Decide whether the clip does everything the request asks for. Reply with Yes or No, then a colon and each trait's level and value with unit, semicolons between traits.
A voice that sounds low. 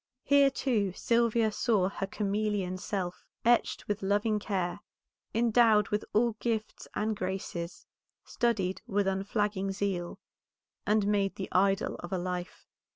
No: high, 205 Hz